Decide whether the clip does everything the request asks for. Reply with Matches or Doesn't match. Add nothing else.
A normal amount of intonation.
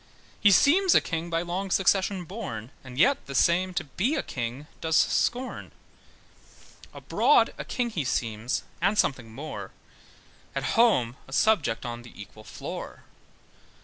Doesn't match